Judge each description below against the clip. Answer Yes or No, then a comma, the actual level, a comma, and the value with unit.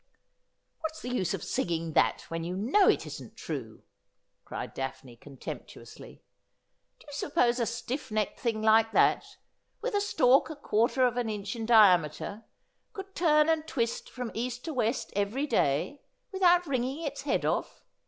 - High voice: Yes, high, 240 Hz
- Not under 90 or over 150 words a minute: No, average, 175 wpm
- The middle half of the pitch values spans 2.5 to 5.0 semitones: No, wide, 5.6 semitones